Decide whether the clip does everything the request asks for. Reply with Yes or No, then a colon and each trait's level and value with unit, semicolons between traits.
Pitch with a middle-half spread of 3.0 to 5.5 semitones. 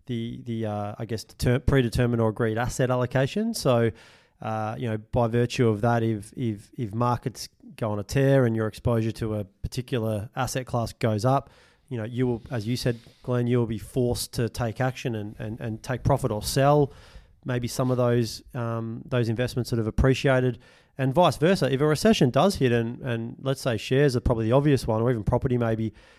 No: narrow, 2.5 semitones